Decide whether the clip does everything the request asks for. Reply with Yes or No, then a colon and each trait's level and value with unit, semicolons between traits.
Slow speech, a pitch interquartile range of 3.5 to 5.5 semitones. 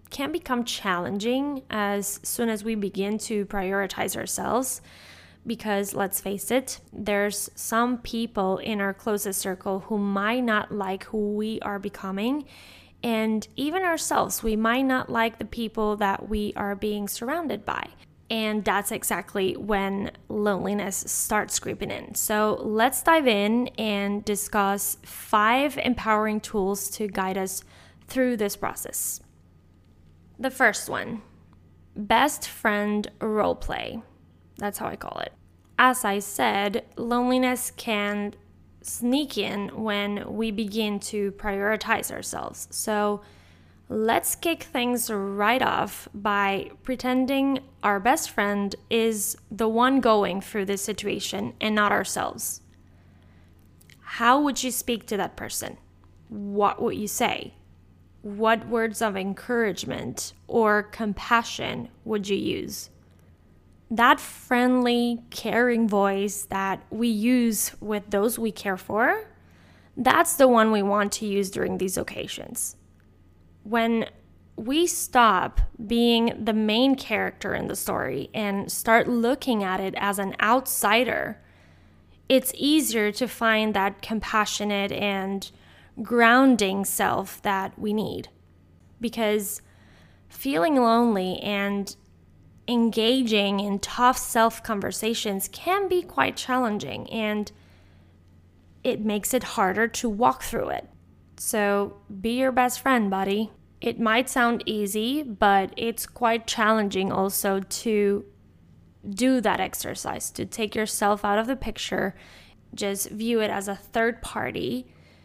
No: slow, 125 wpm; average, 2.8 semitones